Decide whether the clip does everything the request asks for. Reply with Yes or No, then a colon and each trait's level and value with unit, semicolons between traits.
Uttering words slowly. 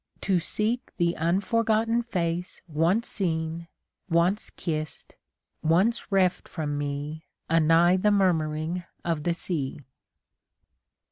Yes: slow, 105 wpm